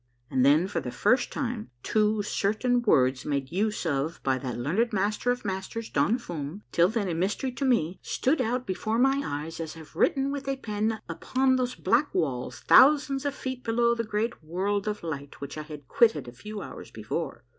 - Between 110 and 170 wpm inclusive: No, fast, 205 wpm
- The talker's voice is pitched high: Yes, high, 210 Hz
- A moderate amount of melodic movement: No, wide, 7.4 semitones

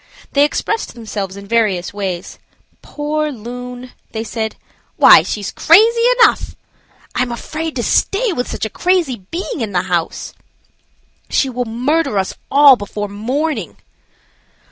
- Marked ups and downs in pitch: Yes, wide, 6.4 semitones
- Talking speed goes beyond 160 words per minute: No, slow, 135 wpm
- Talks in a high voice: Yes, high, 245 Hz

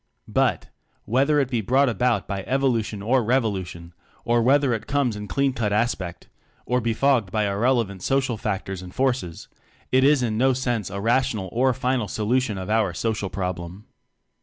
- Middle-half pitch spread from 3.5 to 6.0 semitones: Yes, average, 4.6 semitones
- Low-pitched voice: Yes, low, 115 Hz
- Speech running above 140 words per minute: Yes, average, 180 wpm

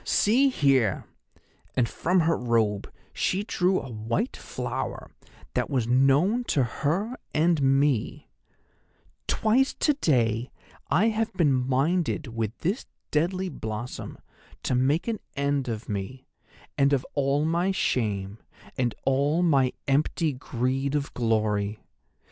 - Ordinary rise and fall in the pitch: No, wide, 6.3 semitones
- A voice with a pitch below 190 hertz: Yes, medium, 140 Hz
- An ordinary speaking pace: No, slow, 120 wpm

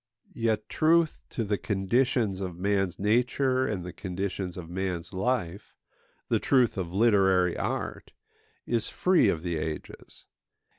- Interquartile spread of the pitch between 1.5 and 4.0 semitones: No, average, 4.4 semitones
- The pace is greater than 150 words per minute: No, slow, 135 wpm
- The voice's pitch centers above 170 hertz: No, low, 100 Hz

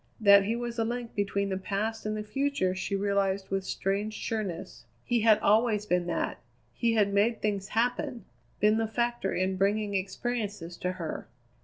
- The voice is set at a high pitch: Yes, high, 210 Hz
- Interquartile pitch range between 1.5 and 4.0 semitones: Yes, narrow, 2.6 semitones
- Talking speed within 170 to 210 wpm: Yes, average, 175 wpm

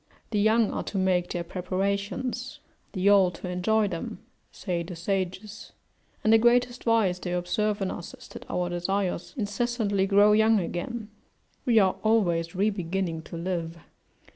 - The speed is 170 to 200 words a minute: No, average, 160 wpm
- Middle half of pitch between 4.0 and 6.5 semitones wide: No, average, 3.4 semitones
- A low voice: No, high, 195 Hz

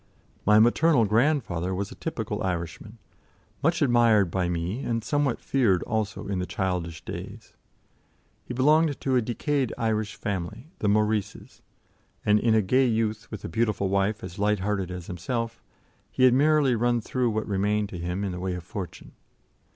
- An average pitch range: Yes, average, 4.0 semitones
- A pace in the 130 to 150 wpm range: No, average, 170 wpm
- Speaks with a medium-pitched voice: No, low, 105 Hz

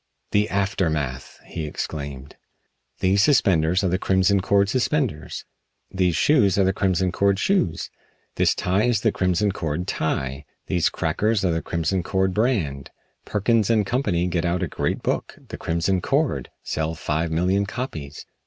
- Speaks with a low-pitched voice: Yes, very low, 95 Hz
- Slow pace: No, average, 155 wpm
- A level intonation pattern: No, average, 3.8 semitones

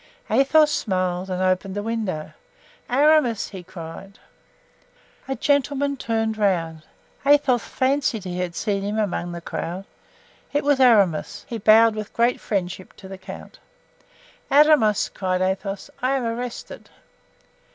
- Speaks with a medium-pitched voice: No, high, 215 Hz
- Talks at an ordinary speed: No, slow, 130 wpm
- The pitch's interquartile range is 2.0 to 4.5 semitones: No, average, 5.3 semitones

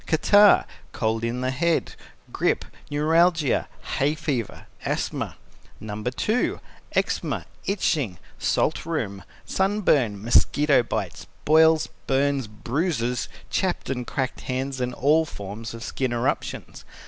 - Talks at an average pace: No, slow, 110 wpm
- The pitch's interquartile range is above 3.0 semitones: Yes, wide, 5.4 semitones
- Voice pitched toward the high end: No, low, 135 Hz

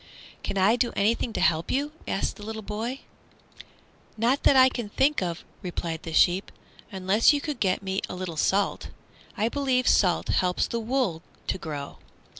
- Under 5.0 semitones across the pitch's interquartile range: No, wide, 5.4 semitones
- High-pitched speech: Yes, high, 205 Hz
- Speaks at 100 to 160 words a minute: No, average, 170 wpm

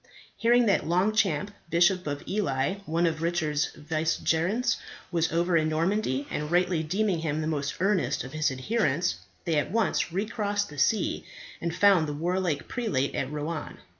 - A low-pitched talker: No, medium, 170 Hz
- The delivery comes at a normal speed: Yes, average, 160 wpm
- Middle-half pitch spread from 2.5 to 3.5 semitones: No, average, 4.3 semitones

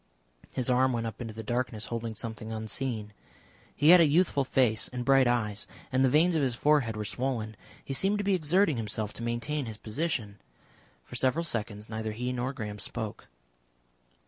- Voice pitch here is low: Yes, low, 120 Hz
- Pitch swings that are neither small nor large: Yes, average, 3.8 semitones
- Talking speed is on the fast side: No, average, 185 wpm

